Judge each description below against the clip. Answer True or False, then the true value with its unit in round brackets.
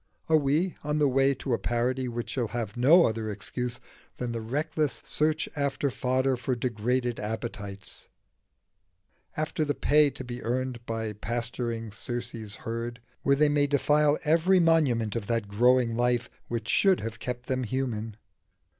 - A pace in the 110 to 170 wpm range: True (155 wpm)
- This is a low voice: True (125 Hz)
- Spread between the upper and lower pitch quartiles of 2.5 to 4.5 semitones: True (3.6 semitones)